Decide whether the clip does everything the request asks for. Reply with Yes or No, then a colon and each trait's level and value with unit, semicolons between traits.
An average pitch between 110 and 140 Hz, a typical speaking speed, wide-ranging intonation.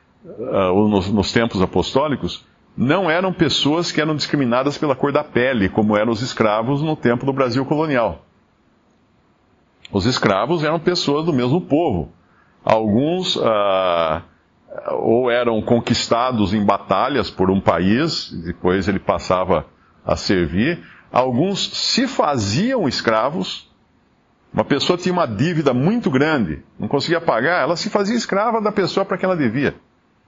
Yes: low, 135 Hz; average, 140 wpm; wide, 8.5 semitones